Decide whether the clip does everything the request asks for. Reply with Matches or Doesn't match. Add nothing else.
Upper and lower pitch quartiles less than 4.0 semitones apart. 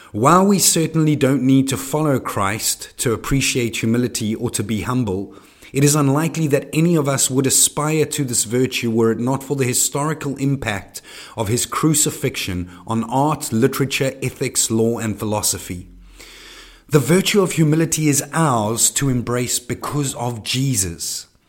Doesn't match